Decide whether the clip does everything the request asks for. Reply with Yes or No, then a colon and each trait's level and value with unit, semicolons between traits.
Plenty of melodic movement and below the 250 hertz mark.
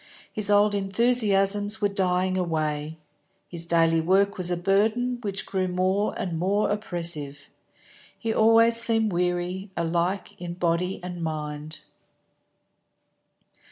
No: average, 3.3 semitones; medium, 185 Hz